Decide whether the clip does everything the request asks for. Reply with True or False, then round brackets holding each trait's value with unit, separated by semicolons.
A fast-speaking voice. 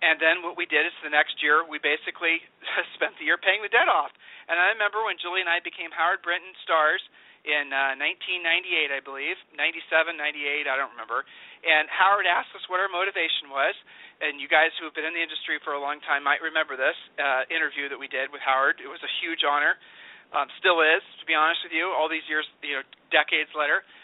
True (225 wpm)